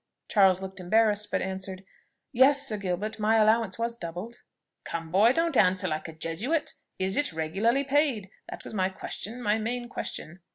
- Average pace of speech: Yes, average, 170 wpm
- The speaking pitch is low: No, high, 210 Hz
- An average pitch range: Yes, average, 4.0 semitones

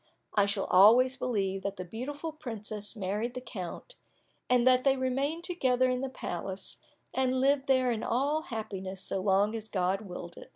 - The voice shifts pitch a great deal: No, average, 4.7 semitones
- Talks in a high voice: Yes, high, 230 Hz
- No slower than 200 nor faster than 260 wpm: No, average, 175 wpm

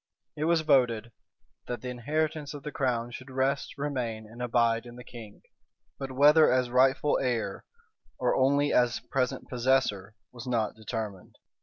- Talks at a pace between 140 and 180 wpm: Yes, average, 160 wpm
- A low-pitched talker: Yes, low, 125 Hz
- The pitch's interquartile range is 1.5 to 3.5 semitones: Yes, average, 3.0 semitones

